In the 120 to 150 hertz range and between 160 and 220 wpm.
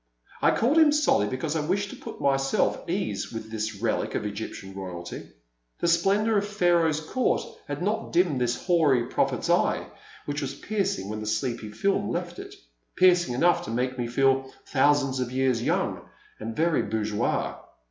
Yes: low, 135 Hz; average, 180 wpm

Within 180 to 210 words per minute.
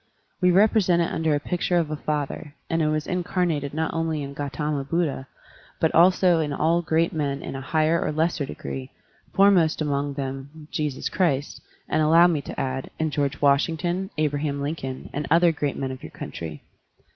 Yes: average, 185 wpm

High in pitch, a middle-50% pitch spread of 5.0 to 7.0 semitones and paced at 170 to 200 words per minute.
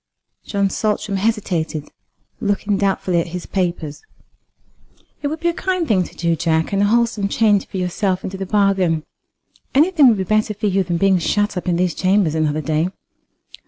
No: high, 195 Hz; average, 3.5 semitones; average, 185 wpm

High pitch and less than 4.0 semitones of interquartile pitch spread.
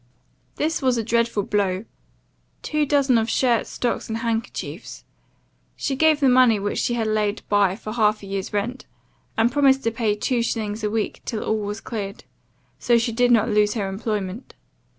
Yes: high, 225 Hz; average, 2.9 semitones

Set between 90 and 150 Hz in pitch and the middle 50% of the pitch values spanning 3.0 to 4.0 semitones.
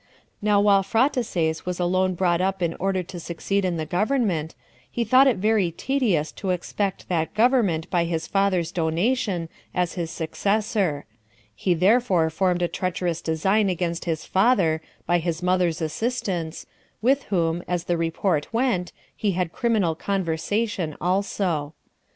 No: medium, 180 Hz; average, 3.5 semitones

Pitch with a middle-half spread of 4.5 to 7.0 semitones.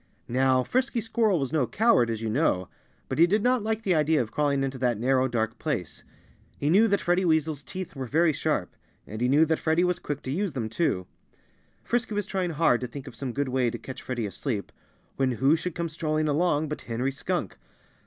Yes: wide, 5.5 semitones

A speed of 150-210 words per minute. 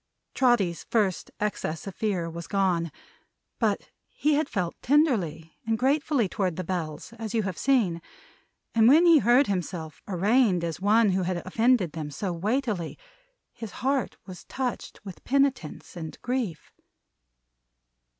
No: average, 140 wpm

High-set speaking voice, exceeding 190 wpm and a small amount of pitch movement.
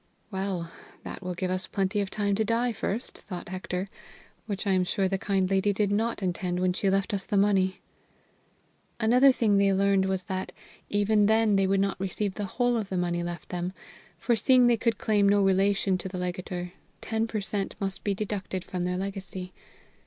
Yes: high, 195 Hz; average, 200 wpm; narrow, 1.9 semitones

